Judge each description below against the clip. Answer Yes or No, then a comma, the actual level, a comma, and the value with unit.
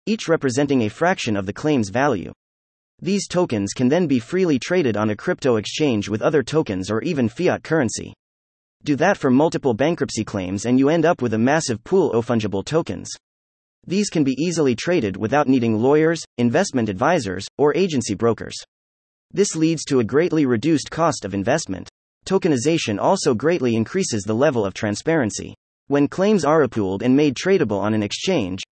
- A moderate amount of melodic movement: No, wide, 7.7 semitones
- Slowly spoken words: No, average, 175 wpm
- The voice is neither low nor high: No, low, 125 Hz